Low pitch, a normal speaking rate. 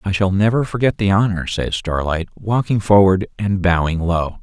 Yes: very low, 95 Hz; average, 175 wpm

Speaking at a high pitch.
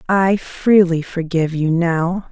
No: medium, 175 Hz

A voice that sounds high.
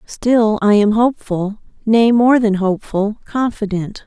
Yes: high, 215 Hz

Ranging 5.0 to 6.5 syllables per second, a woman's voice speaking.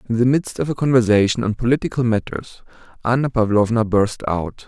No: 5.7 syllables/s; male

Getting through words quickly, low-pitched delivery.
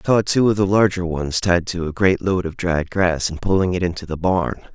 Yes: fast, 265 wpm; very low, 90 Hz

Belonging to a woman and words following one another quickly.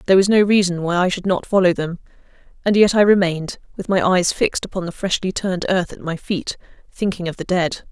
Yes: female; fast, 230 wpm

